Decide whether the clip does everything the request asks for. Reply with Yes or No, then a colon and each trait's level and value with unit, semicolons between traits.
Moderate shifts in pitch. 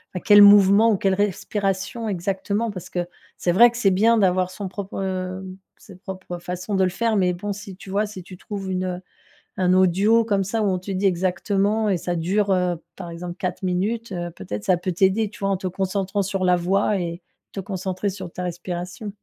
No: narrow, 2.0 semitones